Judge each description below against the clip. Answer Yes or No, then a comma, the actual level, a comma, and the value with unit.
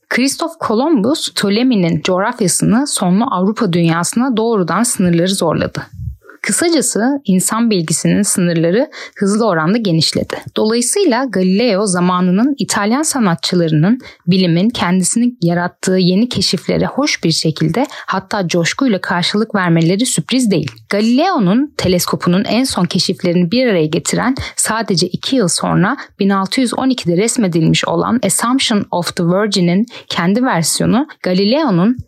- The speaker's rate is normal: Yes, average, 110 wpm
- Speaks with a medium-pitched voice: No, high, 200 Hz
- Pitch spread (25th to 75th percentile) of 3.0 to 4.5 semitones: No, average, 5.1 semitones